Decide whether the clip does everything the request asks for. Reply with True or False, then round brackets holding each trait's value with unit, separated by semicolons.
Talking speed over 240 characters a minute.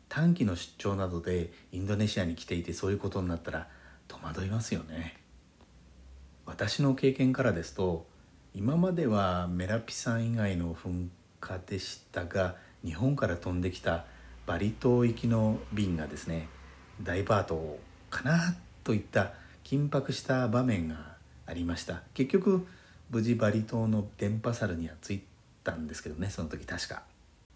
True (300 characters per minute)